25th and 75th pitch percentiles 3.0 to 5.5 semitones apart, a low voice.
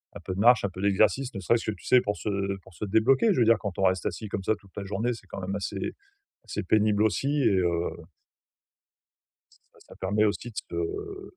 Yes: average, 3.5 semitones; low, 105 Hz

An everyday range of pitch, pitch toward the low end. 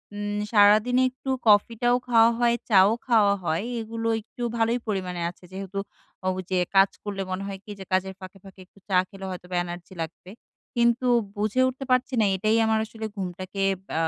No: average, 3.3 semitones; high, 205 Hz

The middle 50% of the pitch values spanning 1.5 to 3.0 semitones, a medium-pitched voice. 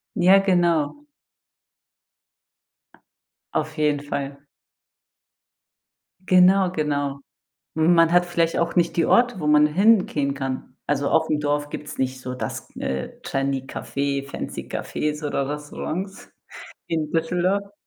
No: average, 3.7 semitones; medium, 150 Hz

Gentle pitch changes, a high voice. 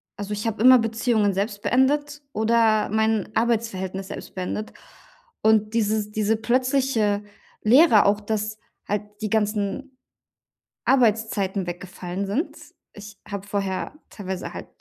Yes: narrow, 2.1 semitones; high, 215 Hz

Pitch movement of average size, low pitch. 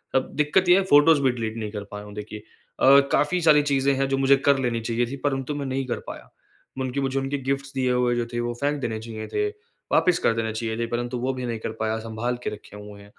Yes: average, 3.6 semitones; low, 125 Hz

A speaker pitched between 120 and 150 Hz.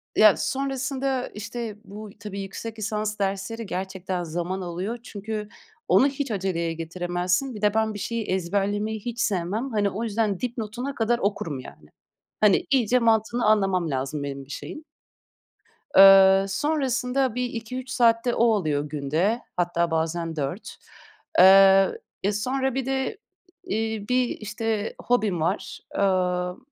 No: high, 210 Hz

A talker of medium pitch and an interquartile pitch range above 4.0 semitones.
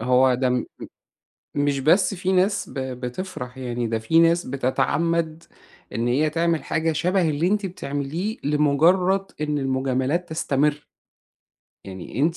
Yes: medium, 150 Hz; average, 4.5 semitones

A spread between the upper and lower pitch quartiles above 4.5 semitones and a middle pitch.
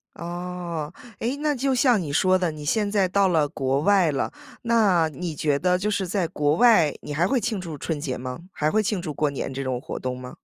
Yes: wide, 5.4 semitones; medium, 175 Hz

